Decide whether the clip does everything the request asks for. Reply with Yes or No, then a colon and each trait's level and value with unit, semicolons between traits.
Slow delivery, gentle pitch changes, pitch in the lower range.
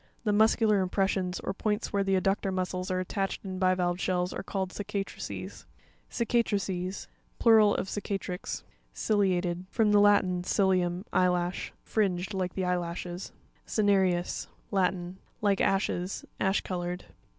No: slow, 120 wpm; narrow, 2.1 semitones; high, 190 Hz